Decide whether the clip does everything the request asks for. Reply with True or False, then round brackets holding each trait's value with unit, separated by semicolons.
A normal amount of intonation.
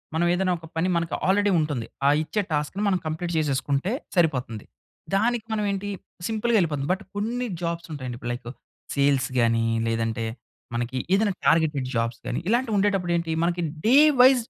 False (7.2 semitones)